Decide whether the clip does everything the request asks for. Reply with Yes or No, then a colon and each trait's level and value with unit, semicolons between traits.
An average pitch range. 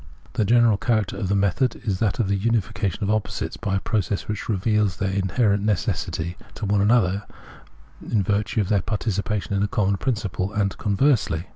No: narrow, 2.0 semitones